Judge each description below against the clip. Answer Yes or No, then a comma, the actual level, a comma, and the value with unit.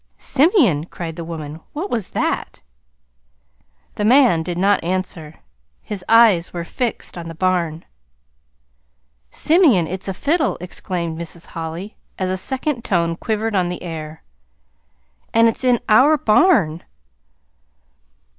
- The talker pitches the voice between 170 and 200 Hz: Yes, medium, 185 Hz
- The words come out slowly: Yes, slow, 125 wpm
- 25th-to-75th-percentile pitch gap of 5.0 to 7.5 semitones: Yes, wide, 5.6 semitones